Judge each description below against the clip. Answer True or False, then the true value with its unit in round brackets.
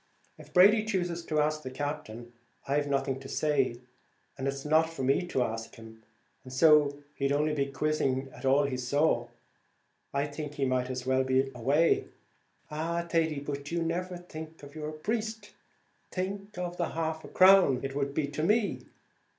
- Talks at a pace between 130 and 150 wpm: False (170 wpm)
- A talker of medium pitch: True (150 Hz)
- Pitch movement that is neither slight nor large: True (3.7 semitones)